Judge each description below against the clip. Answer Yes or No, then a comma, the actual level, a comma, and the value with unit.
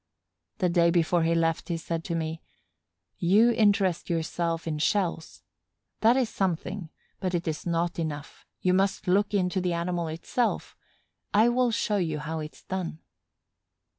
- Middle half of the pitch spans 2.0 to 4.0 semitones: Yes, average, 3.0 semitones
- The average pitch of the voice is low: No, medium, 175 Hz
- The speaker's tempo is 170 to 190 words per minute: No, average, 155 wpm